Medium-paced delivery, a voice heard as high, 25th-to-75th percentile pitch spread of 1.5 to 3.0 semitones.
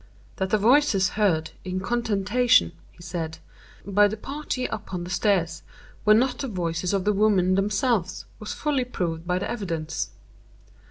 No: average, 155 wpm; high, 195 Hz; average, 3.8 semitones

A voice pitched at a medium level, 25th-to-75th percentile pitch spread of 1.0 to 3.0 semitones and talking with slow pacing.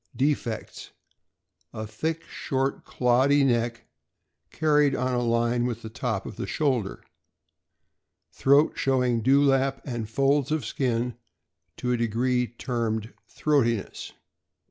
No: low, 125 Hz; average, 2.7 semitones; slow, 115 wpm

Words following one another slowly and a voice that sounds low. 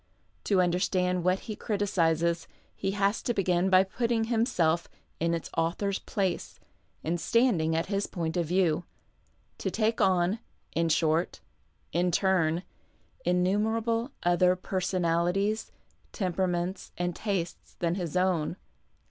No: slow, 125 wpm; medium, 180 Hz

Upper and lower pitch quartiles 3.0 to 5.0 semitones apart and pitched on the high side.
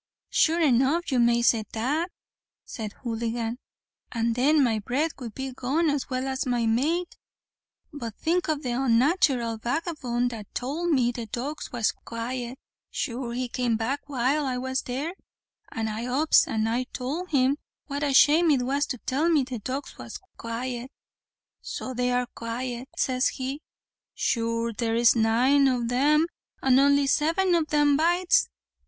Yes: average, 3.6 semitones; very high, 255 Hz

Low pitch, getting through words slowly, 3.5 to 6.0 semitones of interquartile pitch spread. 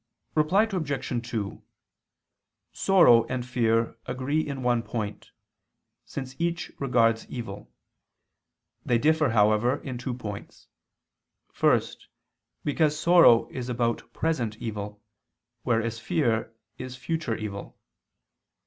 Yes: low, 125 Hz; slow, 105 wpm; average, 4.3 semitones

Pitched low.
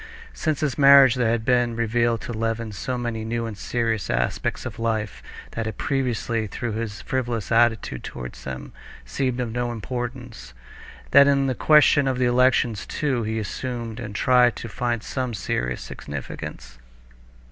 Yes: low, 120 Hz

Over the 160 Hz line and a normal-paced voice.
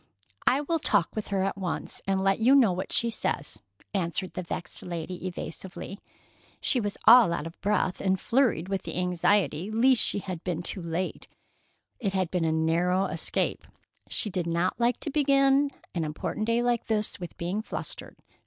Yes: high, 190 Hz; average, 180 wpm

